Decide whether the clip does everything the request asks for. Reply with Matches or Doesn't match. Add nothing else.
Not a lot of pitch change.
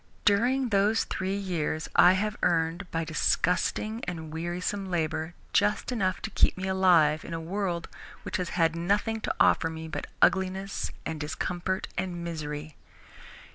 Doesn't match